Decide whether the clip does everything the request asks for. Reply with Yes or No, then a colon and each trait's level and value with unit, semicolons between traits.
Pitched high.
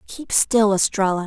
Yes: high, 200 Hz